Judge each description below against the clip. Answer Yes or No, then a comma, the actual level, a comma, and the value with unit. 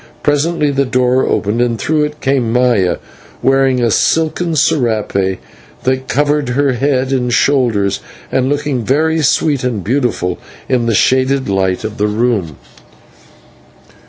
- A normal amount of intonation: Yes, average, 4.0 semitones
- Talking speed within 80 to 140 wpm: Yes, slow, 135 wpm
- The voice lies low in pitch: Yes, low, 130 Hz